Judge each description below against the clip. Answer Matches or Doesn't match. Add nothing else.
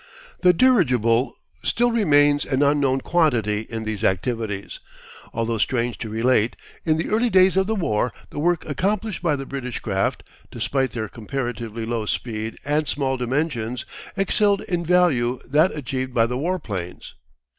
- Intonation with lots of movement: Matches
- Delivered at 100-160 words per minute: Matches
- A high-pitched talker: Doesn't match